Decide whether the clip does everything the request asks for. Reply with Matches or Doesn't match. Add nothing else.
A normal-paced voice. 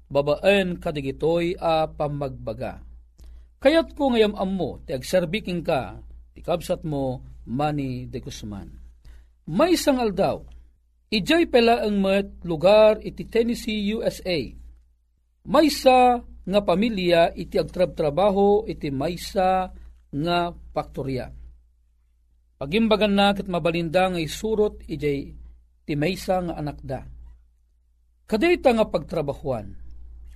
Doesn't match